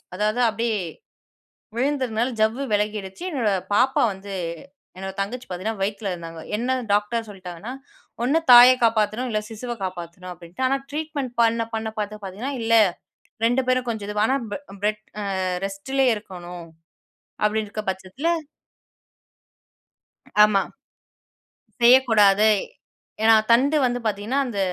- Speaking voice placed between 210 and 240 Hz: Yes, high, 215 Hz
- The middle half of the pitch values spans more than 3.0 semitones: Yes, average, 3.7 semitones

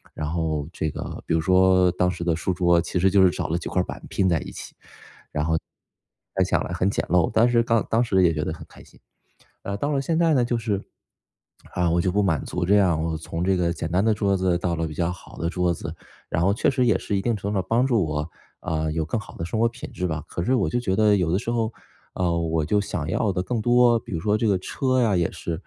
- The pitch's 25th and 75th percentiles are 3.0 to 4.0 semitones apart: No, average, 4.5 semitones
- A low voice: Yes, very low, 90 Hz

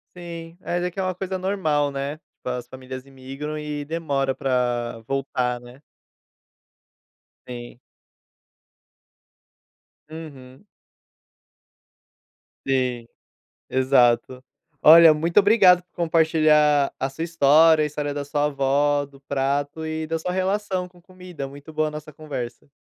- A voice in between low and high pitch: Yes, medium, 150 Hz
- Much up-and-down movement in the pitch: No, average, 3.5 semitones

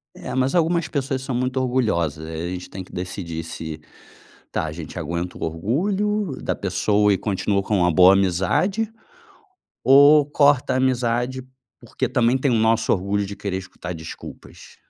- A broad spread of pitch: Yes, wide, 6.4 semitones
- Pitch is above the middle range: No, low, 110 Hz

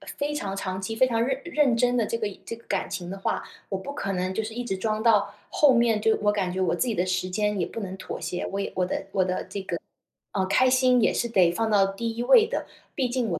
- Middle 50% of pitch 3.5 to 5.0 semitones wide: Yes, average, 4.0 semitones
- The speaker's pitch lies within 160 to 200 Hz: No, high, 210 Hz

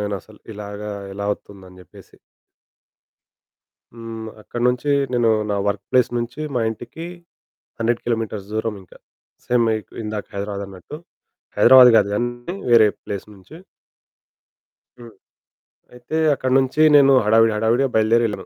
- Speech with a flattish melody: No, average, 3.0 semitones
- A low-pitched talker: Yes, low, 115 Hz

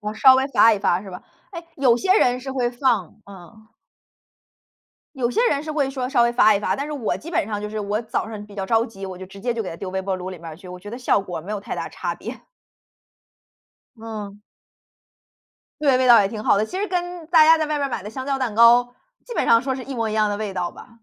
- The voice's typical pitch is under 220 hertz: No, high, 230 Hz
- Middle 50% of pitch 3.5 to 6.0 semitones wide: Yes, average, 4.6 semitones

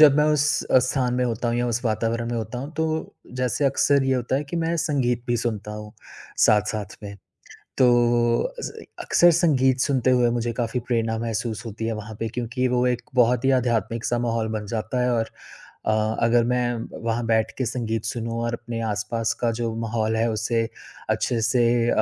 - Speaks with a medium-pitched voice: No, low, 120 Hz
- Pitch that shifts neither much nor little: No, narrow, 1.9 semitones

